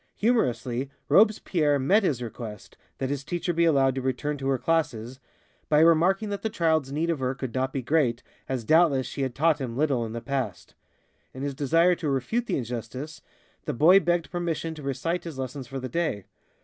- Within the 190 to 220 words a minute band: Yes, average, 200 wpm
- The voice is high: No, medium, 140 Hz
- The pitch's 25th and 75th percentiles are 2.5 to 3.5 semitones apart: No, average, 4.3 semitones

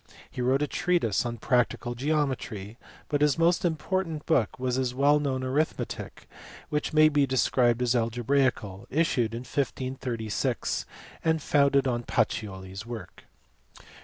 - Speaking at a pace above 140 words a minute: No, slow, 135 wpm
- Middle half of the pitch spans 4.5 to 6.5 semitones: No, average, 3.8 semitones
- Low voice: Yes, low, 130 Hz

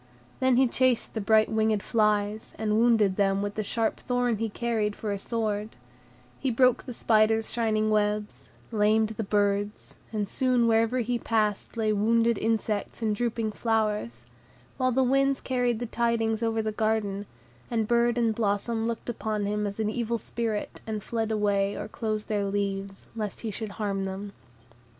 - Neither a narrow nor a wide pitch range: No, narrow, 1.9 semitones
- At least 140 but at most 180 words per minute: Yes, average, 170 wpm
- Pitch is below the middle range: No, high, 220 Hz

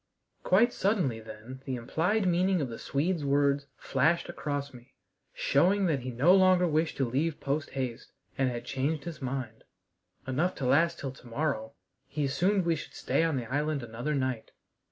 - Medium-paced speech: Yes, average, 175 wpm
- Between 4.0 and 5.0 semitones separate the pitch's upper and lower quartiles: Yes, average, 4.5 semitones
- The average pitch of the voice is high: No, medium, 140 Hz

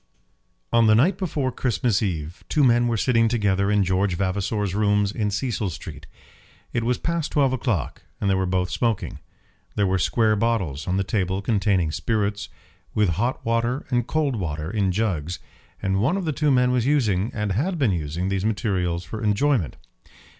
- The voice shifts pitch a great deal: No, average, 4.3 semitones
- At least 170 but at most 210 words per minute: Yes, average, 180 wpm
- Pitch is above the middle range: No, low, 105 Hz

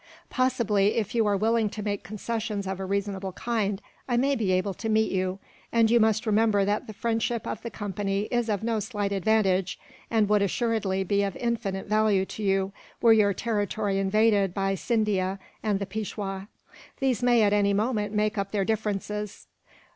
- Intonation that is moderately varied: No, narrow, 2.2 semitones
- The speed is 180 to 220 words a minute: Yes, average, 185 wpm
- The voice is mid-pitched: No, high, 210 Hz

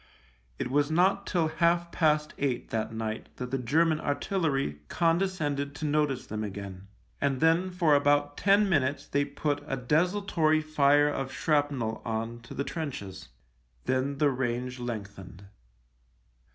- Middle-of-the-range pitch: Yes, medium, 145 Hz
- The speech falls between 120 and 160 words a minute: Yes, average, 140 wpm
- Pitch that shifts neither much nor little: Yes, average, 4.2 semitones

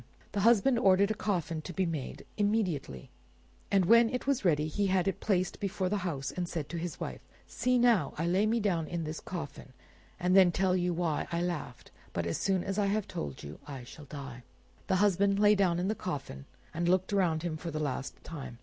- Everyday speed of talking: No, fast, 220 wpm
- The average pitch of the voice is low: No, medium, 180 Hz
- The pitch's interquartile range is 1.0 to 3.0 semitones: No, average, 4.3 semitones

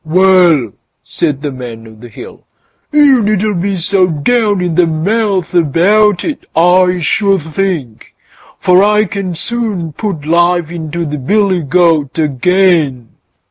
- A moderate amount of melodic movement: Yes, average, 4.2 semitones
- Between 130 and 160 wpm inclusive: Yes, average, 140 wpm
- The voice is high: No, medium, 175 Hz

